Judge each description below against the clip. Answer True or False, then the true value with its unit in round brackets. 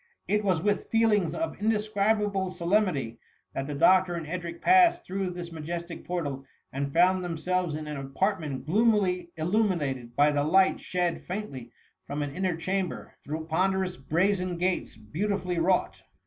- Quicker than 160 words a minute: False (155 wpm)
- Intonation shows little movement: False (3.8 semitones)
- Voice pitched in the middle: True (180 Hz)